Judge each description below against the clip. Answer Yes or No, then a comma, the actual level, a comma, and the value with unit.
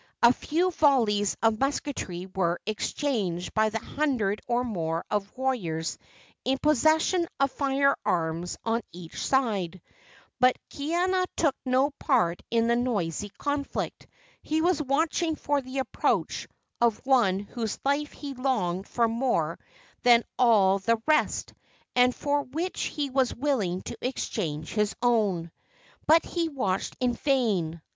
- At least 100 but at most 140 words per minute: Yes, slow, 135 wpm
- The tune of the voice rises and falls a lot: Yes, wide, 6.2 semitones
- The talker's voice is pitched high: Yes, high, 245 Hz